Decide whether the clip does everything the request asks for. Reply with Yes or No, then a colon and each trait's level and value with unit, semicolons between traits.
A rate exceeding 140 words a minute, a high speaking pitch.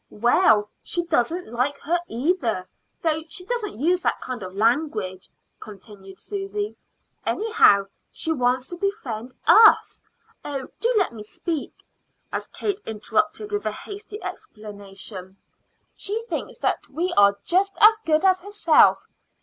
No: slow, 135 wpm; very high, 310 Hz